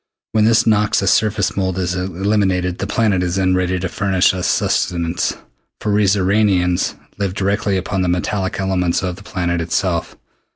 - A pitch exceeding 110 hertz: No, very low, 95 Hz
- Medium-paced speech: Yes, average, 165 wpm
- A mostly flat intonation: Yes, narrow, 1.9 semitones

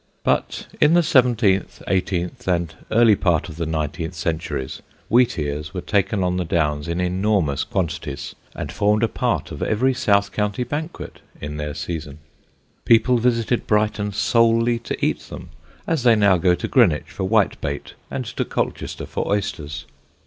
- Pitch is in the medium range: No, very low, 95 Hz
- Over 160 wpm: No, average, 155 wpm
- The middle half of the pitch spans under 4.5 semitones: No, wide, 5.5 semitones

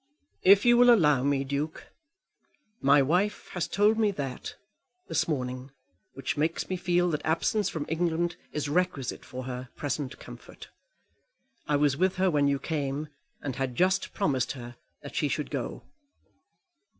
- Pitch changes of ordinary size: Yes, average, 4.7 semitones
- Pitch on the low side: No, medium, 150 Hz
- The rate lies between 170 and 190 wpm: No, average, 155 wpm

